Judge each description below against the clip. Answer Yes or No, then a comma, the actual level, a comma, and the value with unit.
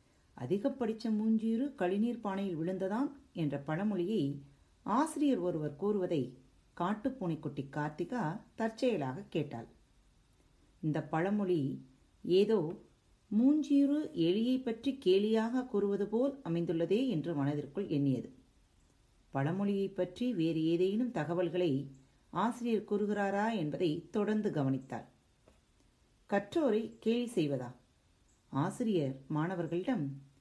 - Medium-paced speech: Yes, average, 85 wpm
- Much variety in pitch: Yes, wide, 6.7 semitones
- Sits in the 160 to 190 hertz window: Yes, medium, 185 Hz